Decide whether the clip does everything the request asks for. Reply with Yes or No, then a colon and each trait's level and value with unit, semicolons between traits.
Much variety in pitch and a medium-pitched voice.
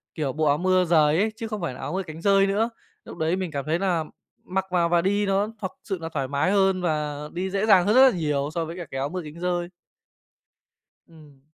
No: average, 3.8 semitones; medium, 175 Hz